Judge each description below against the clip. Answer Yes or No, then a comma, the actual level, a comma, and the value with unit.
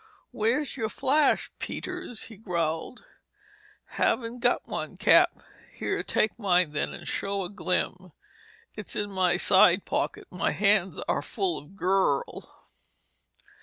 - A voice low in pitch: No, high, 200 Hz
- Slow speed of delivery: Yes, slow, 125 wpm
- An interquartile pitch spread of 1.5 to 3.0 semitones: No, average, 4.0 semitones